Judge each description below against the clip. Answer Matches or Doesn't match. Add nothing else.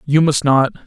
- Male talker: Matches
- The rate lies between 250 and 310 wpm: Doesn't match